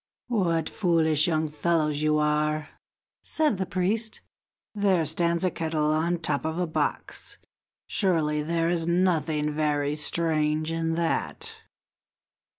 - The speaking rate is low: Yes, slow, 130 wpm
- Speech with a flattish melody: Yes, narrow, 2.2 semitones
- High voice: No, medium, 160 Hz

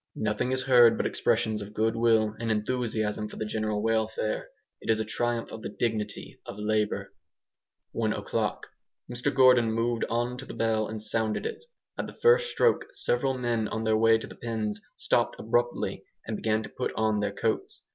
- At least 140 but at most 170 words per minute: No, average, 185 wpm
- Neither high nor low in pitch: No, low, 110 Hz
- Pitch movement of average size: No, narrow, 1.8 semitones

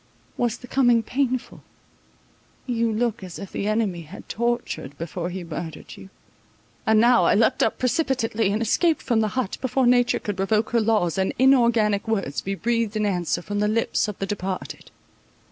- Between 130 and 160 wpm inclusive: No, average, 180 wpm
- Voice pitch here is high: Yes, high, 220 Hz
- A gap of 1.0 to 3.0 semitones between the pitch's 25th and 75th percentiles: No, average, 3.6 semitones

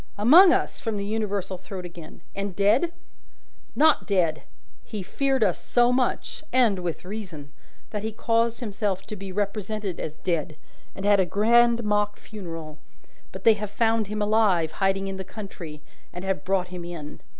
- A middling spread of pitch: Yes, average, 3.3 semitones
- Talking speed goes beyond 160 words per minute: Yes, average, 170 wpm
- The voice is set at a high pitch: Yes, high, 200 Hz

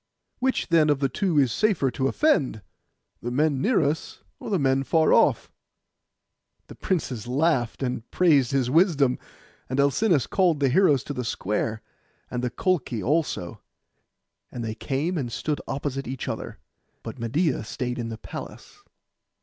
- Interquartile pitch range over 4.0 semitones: Yes, average, 4.7 semitones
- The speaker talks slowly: No, average, 160 wpm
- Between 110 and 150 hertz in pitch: Yes, low, 135 Hz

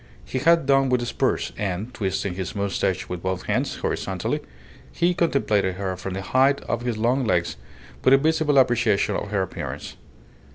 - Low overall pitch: Yes, low, 115 Hz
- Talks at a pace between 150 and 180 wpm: Yes, average, 175 wpm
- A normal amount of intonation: No, wide, 6.0 semitones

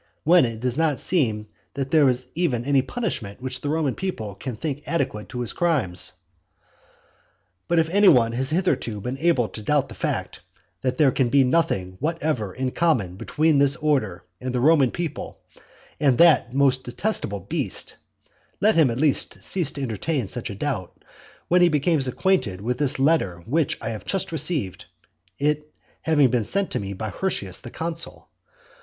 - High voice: No, low, 135 Hz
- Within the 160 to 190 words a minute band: Yes, average, 175 wpm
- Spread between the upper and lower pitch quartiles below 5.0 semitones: No, wide, 5.6 semitones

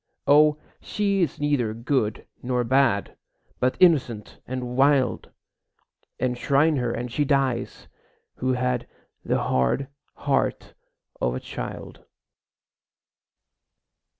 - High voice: No, low, 130 Hz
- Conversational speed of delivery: No, slow, 100 wpm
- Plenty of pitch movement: No, average, 3.0 semitones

